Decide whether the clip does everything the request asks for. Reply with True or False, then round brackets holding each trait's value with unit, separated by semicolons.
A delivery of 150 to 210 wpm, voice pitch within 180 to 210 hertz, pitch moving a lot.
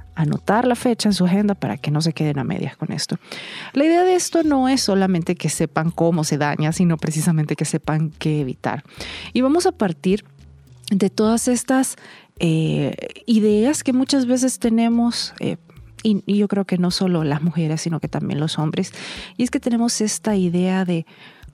True (190 wpm; 185 Hz; 6.6 semitones)